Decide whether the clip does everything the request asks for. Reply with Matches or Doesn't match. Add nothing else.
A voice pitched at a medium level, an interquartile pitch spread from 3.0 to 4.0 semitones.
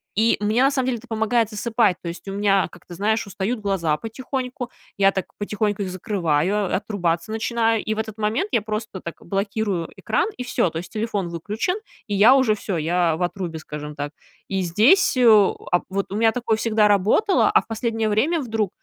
Doesn't match